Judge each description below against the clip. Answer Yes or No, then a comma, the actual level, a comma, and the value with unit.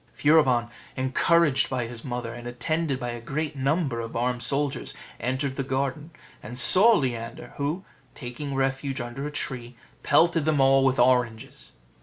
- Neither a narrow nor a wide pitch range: Yes, average, 3.2 semitones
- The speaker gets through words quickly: No, average, 155 wpm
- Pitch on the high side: No, low, 130 Hz